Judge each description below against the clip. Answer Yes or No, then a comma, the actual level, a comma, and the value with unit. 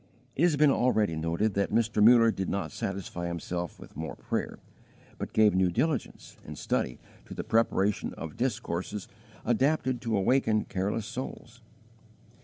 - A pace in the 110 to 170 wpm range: Yes, average, 150 wpm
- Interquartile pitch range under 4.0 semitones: No, average, 4.6 semitones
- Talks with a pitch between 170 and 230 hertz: No, low, 105 Hz